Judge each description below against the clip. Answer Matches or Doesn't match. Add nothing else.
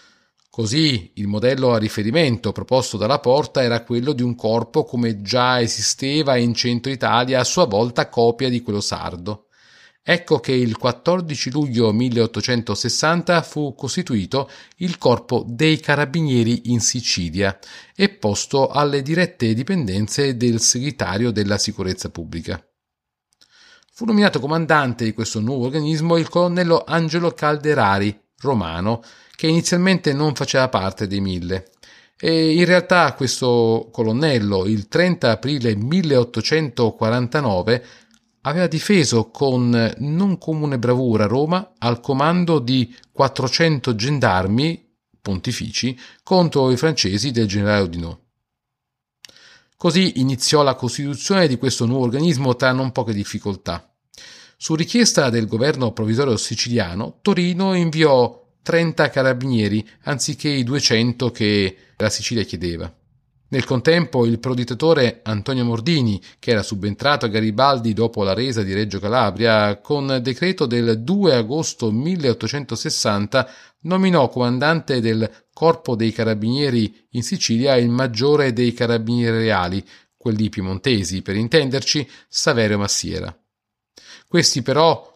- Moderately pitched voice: Doesn't match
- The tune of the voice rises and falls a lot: Doesn't match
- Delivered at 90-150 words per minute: Matches